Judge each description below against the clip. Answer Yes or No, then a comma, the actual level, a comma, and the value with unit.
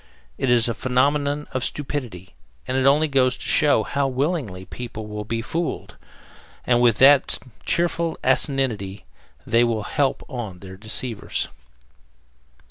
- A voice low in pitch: Yes, low, 125 Hz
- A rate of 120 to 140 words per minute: Yes, slow, 135 wpm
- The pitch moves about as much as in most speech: Yes, average, 4.4 semitones